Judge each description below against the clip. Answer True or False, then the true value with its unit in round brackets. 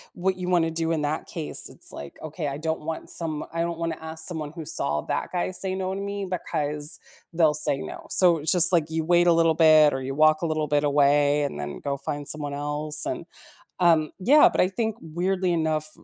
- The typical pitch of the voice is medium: True (160 Hz)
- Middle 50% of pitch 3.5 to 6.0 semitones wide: False (2.7 semitones)